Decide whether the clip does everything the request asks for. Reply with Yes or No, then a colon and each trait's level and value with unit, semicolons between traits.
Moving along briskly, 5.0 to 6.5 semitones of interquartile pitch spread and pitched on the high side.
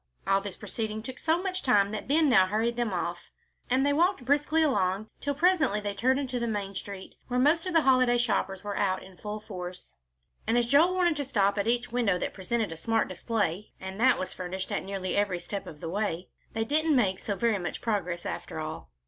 Yes: fast, 225 wpm; wide, 5.4 semitones; high, 215 Hz